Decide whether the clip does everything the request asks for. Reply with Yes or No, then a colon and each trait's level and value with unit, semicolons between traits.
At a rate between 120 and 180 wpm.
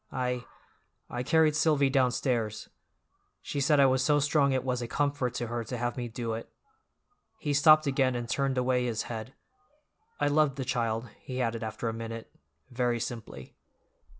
Yes: average, 170 wpm